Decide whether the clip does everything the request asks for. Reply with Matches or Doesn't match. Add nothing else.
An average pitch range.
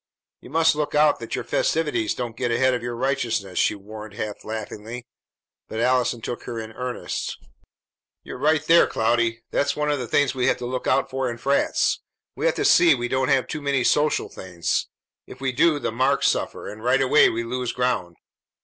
Matches